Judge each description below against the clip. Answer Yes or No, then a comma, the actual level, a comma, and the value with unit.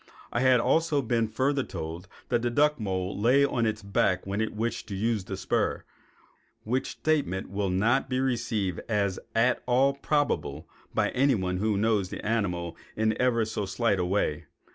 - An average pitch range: Yes, average, 4.5 semitones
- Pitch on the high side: No, low, 110 Hz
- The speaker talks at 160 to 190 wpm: Yes, average, 175 wpm